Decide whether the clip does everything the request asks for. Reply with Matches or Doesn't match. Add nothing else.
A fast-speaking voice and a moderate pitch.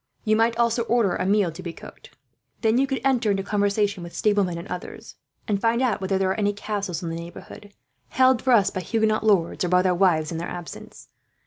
Doesn't match